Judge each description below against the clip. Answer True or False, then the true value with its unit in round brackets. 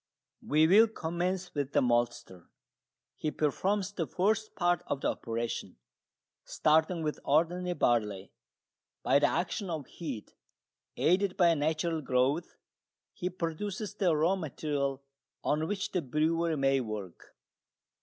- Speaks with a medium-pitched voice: True (160 Hz)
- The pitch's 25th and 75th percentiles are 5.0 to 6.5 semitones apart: False (4.6 semitones)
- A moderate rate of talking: False (125 wpm)